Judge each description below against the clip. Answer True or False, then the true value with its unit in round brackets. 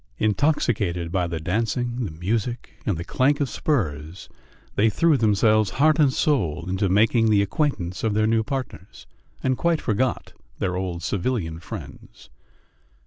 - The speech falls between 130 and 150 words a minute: True (145 wpm)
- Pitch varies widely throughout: True (5.9 semitones)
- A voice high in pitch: False (110 Hz)